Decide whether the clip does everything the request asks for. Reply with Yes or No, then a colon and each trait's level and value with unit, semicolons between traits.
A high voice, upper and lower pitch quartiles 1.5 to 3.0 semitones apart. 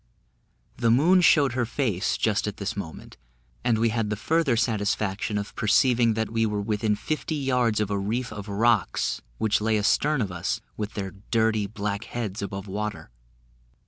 No: low, 110 Hz; narrow, 2.6 semitones